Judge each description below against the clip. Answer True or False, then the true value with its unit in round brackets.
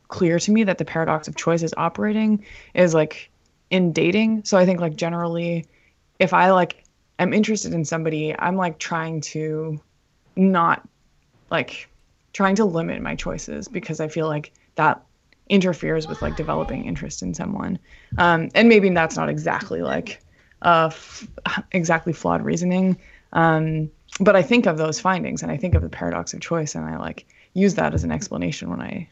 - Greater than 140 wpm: True (180 wpm)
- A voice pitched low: False (170 Hz)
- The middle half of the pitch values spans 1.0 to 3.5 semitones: True (2.9 semitones)